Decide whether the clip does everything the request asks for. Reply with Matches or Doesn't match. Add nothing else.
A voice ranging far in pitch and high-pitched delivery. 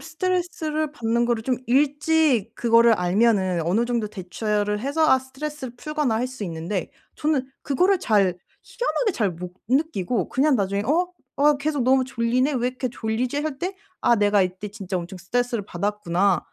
Matches